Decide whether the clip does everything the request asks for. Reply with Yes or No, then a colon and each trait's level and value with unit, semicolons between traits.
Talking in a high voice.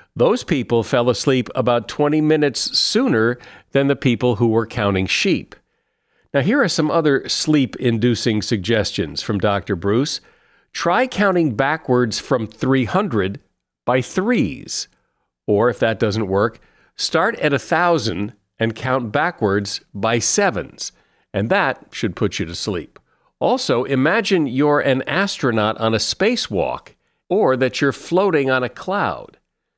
No: low, 125 Hz